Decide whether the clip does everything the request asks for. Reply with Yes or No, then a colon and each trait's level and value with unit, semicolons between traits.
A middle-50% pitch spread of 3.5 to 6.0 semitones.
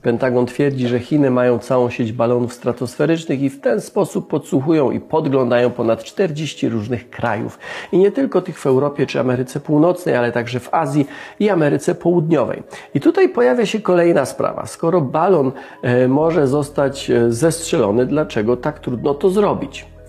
Yes: average, 5.1 semitones